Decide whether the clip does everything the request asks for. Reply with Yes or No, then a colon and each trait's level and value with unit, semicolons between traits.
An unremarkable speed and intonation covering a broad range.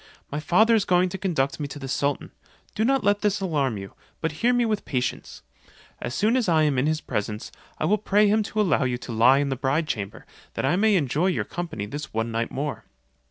No: fast, 235 wpm; wide, 7.4 semitones